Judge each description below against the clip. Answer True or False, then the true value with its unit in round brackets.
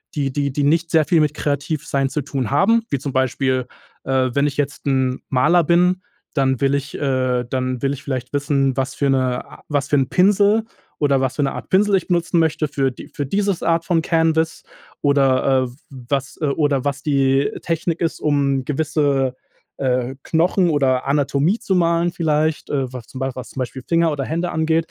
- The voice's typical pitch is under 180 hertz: True (140 Hz)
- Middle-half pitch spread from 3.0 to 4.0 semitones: True (3.4 semitones)